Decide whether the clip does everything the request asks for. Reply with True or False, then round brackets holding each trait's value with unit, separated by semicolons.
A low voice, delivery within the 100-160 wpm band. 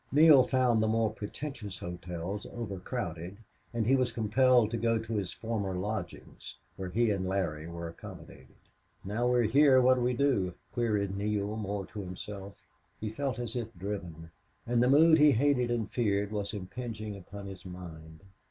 False (105 Hz; 170 wpm)